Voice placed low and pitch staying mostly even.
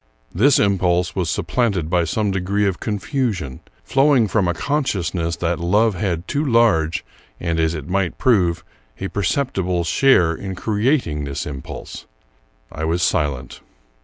No: very low, 90 Hz; average, 4.8 semitones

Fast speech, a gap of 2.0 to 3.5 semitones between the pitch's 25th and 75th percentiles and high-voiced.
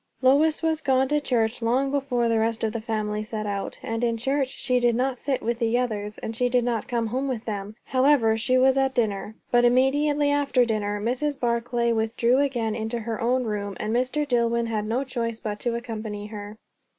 Yes: fast, 210 wpm; average, 2.8 semitones; high, 235 Hz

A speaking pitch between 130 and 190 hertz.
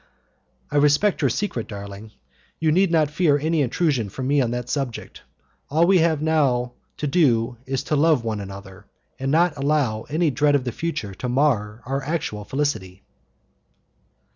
Yes: medium, 140 Hz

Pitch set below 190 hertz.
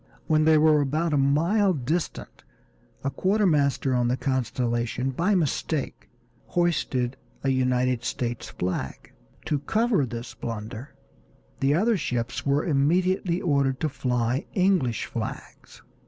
Yes: medium, 140 Hz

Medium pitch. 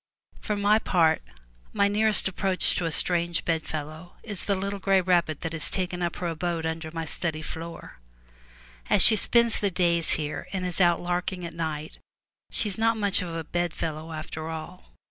Yes: medium, 175 Hz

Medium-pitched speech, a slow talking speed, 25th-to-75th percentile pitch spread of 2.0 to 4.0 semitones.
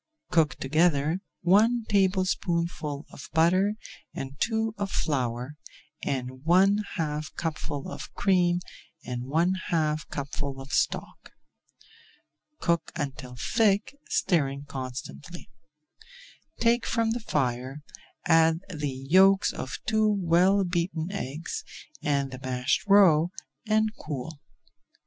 No: medium, 165 Hz; slow, 110 wpm; wide, 5.5 semitones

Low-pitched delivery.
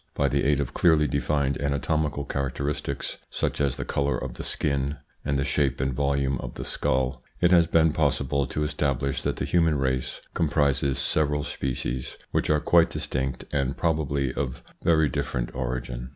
Yes: very low, 70 Hz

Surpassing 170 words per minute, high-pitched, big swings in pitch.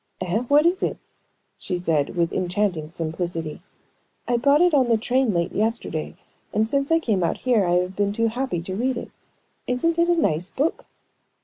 Yes: average, 195 wpm; high, 215 Hz; wide, 7.0 semitones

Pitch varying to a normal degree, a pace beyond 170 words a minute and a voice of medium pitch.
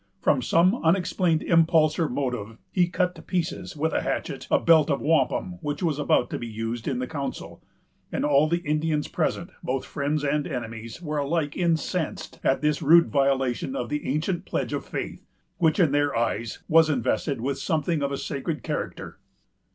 Yes: average, 3.2 semitones; average, 180 wpm; medium, 150 Hz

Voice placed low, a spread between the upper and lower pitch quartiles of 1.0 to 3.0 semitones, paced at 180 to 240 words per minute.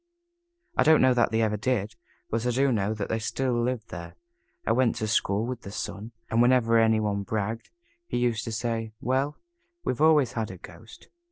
Yes: low, 115 Hz; narrow, 2.6 semitones; average, 200 wpm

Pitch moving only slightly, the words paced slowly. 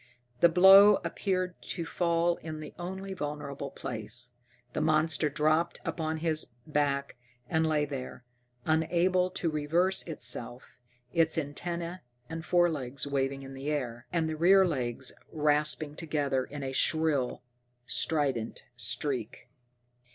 No: average, 3.5 semitones; slow, 125 wpm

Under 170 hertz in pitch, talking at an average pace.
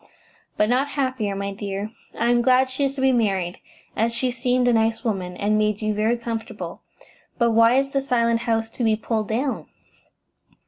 No: high, 230 Hz; average, 190 wpm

